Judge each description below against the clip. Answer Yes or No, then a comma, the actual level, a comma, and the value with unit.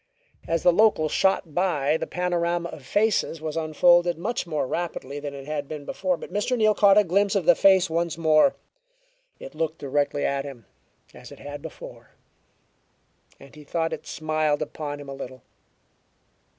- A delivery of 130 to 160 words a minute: No, average, 175 wpm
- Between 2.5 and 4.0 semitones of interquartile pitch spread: Yes, average, 3.6 semitones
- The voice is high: No, medium, 160 Hz